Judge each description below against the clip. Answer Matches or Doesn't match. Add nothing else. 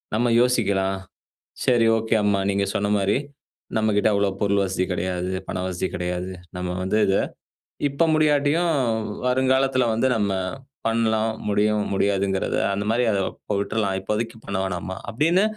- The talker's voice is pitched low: Matches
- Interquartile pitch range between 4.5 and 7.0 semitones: Doesn't match